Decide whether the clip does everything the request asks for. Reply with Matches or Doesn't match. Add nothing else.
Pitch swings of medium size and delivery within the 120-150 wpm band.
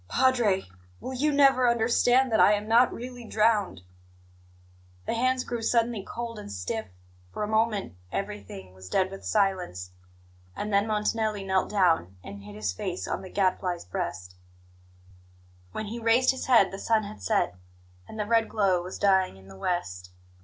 Doesn't match